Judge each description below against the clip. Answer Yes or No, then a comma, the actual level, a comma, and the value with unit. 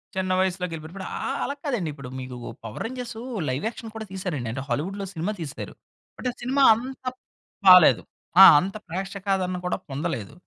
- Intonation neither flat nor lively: No, wide, 5.8 semitones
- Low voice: No, medium, 185 Hz